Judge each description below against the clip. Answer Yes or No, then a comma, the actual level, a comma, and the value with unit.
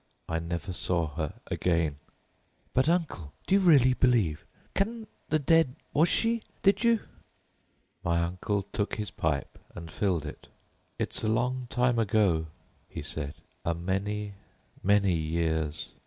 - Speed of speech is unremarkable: No, slow, 130 wpm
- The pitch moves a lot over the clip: Yes, wide, 7.6 semitones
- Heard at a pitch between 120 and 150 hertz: No, low, 100 Hz